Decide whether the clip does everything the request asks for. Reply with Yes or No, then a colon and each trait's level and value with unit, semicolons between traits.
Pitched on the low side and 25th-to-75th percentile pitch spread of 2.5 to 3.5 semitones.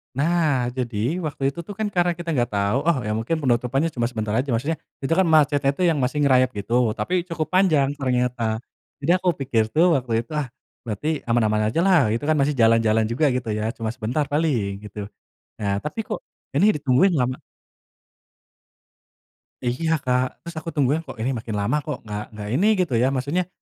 No: low, 130 Hz; wide, 5.5 semitones